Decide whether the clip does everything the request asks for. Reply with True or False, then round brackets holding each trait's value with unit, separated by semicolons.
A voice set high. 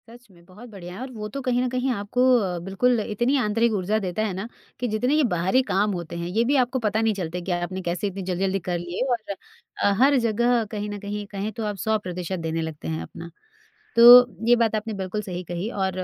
True (205 Hz)